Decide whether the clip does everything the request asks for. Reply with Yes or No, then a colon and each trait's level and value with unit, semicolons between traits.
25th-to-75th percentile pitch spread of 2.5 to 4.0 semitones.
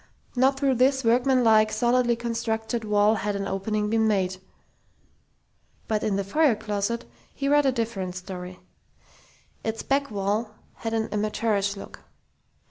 Yes: average, 2.8 semitones